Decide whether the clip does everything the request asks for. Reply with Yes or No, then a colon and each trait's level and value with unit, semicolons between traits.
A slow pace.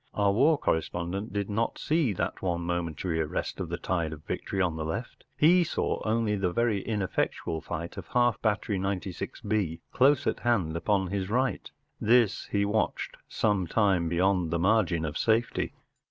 No: average, 170 wpm